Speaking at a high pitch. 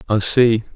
No: low, 115 Hz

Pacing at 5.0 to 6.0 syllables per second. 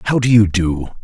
Yes: 5.7 syllables/s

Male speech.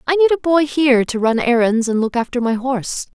No: female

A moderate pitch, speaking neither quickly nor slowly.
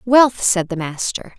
No: high, 205 Hz; average, 175 wpm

